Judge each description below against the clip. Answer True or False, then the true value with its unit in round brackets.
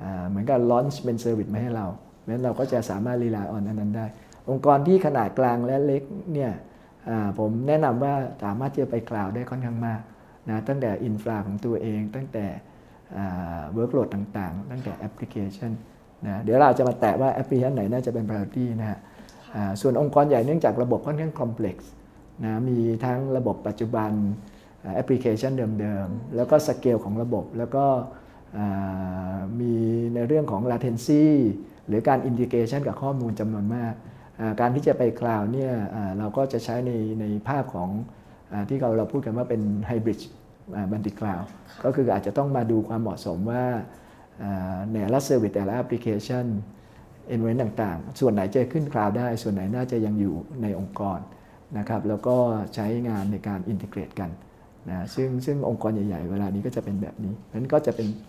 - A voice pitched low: True (115 Hz)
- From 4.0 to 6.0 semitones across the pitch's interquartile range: False (3.3 semitones)